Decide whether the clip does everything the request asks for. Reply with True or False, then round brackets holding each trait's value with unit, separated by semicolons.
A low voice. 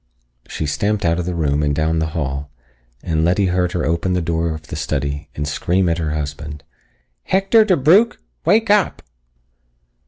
True (85 Hz)